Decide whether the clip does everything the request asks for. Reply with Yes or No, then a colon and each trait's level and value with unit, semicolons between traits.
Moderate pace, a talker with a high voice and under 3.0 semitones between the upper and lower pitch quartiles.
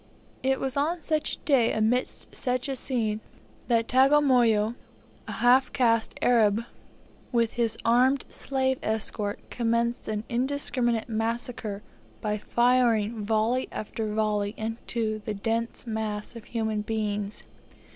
No: slow, 125 wpm; high, 230 Hz; narrow, 2.6 semitones